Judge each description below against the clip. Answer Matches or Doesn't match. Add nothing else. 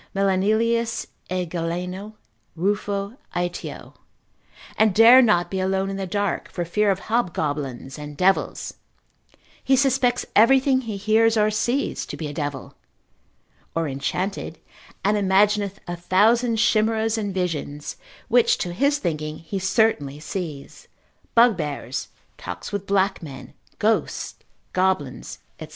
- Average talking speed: Doesn't match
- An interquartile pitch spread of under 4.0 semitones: Doesn't match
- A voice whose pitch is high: Matches